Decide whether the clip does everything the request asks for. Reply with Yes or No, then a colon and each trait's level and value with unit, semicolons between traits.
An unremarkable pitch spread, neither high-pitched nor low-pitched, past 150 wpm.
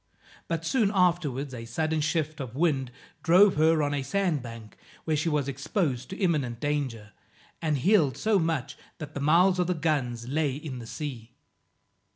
Yes: average, 4.1 semitones; medium, 150 Hz; average, 175 wpm